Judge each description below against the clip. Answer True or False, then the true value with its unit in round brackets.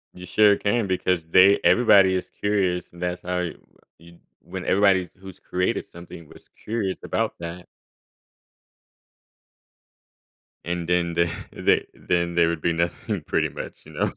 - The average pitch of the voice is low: True (90 Hz)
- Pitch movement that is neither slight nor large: False (1.8 semitones)